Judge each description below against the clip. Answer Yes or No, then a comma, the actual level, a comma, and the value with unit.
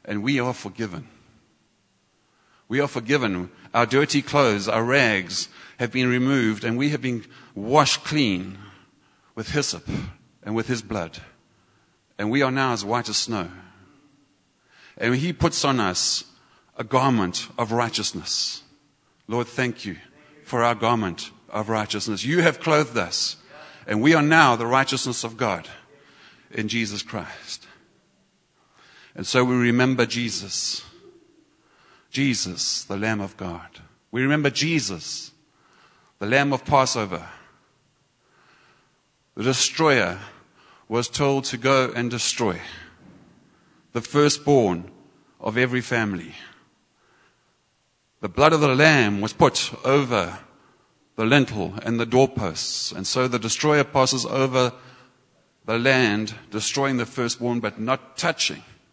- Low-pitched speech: Yes, low, 120 Hz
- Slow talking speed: Yes, slow, 125 wpm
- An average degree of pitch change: Yes, average, 4.1 semitones